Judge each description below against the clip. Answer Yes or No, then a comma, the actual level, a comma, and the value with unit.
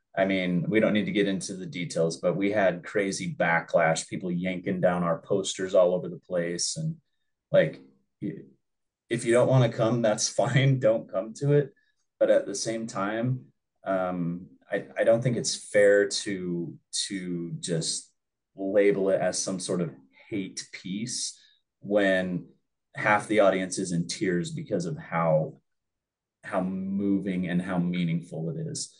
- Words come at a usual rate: Yes, average, 160 wpm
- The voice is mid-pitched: No, very low, 95 Hz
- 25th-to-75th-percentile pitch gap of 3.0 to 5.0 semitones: Yes, average, 4.3 semitones